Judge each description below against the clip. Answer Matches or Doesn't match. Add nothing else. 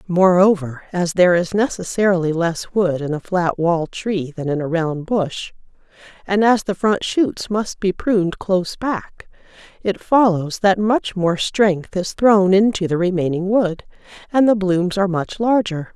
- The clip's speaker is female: Matches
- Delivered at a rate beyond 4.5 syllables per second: Doesn't match